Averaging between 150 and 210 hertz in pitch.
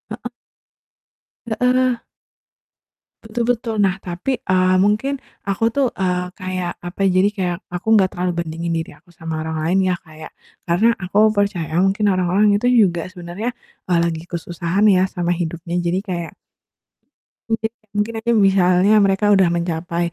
Yes: medium, 185 Hz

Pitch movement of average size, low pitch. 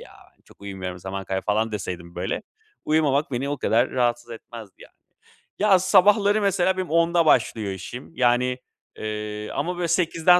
No: wide, 8.5 semitones; low, 125 Hz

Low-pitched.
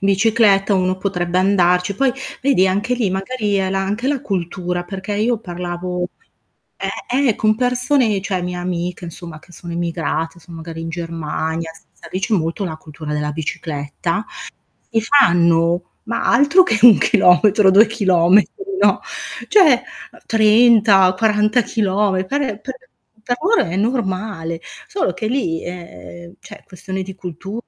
No: high, 190 Hz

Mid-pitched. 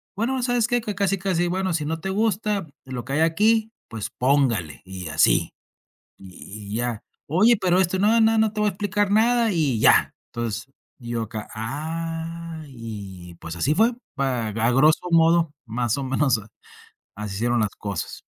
Yes: medium, 160 Hz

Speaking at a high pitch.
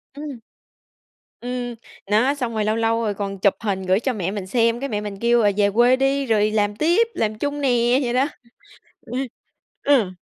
Yes: high, 230 Hz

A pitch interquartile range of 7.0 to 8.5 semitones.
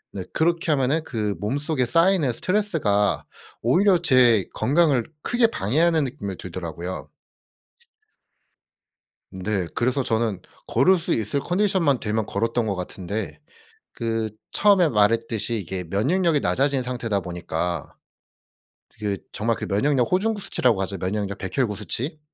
Yes: wide, 7.3 semitones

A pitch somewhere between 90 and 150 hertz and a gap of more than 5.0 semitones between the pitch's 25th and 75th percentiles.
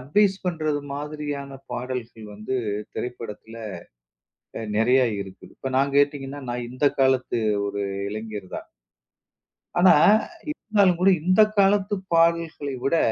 Yes: medium, 140 Hz; wide, 5.5 semitones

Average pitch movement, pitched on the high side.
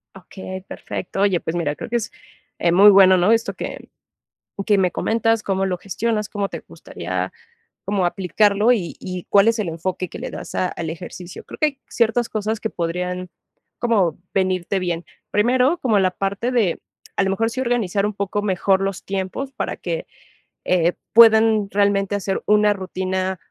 Yes: average, 3.1 semitones; high, 195 Hz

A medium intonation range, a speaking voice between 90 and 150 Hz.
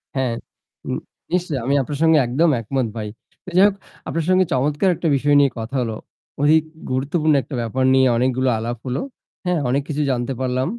Yes: average, 3.6 semitones; low, 135 Hz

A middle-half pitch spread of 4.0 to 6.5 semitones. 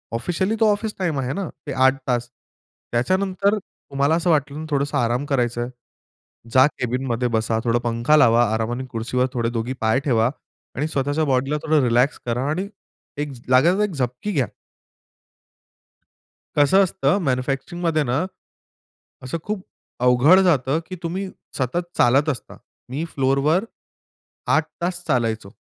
Yes: average, 5.1 semitones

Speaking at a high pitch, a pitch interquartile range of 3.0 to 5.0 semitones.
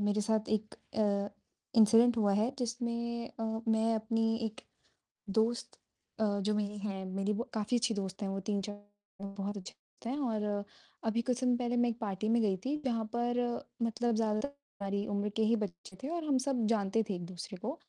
No: high, 220 Hz; narrow, 2.5 semitones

